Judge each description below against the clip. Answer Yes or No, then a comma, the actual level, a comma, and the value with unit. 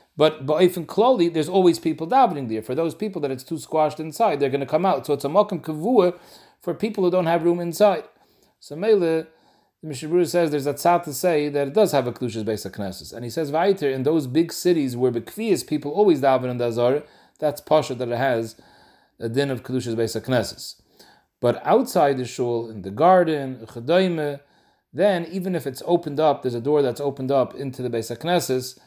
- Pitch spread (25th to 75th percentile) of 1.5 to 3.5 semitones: No, average, 5.2 semitones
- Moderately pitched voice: Yes, medium, 150 Hz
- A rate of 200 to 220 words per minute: Yes, fast, 205 wpm